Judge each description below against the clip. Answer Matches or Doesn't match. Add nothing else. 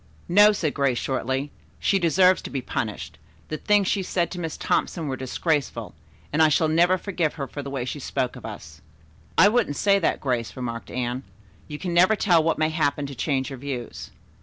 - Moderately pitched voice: Matches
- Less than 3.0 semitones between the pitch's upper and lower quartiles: Doesn't match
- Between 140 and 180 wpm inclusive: Doesn't match